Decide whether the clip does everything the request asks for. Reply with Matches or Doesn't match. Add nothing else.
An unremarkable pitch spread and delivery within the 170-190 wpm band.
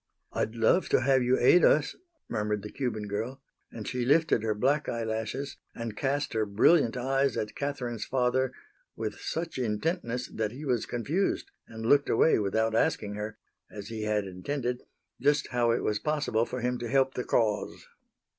Matches